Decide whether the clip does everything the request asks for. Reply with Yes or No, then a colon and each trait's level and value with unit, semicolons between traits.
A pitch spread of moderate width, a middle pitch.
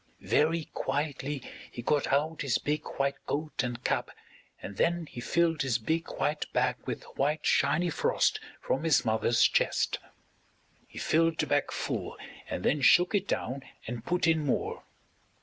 Yes: average, 3.7 semitones; medium, 145 Hz